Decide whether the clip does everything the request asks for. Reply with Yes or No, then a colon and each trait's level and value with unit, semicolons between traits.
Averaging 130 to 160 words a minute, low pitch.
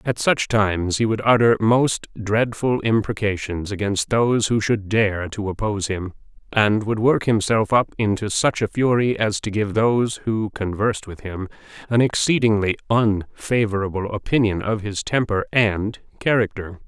Yes: average, 155 wpm; low, 105 Hz